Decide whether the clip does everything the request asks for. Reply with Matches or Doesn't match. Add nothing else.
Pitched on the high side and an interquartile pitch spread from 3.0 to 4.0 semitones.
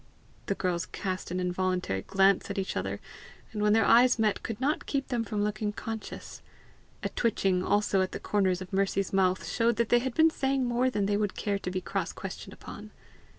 Matches